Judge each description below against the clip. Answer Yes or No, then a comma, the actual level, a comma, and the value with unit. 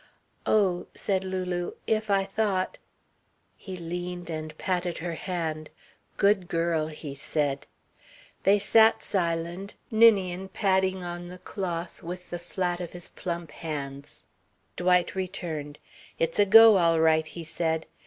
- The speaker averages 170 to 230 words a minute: No, slow, 135 wpm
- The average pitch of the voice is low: No, medium, 175 Hz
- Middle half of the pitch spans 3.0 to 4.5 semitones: No, narrow, 2.5 semitones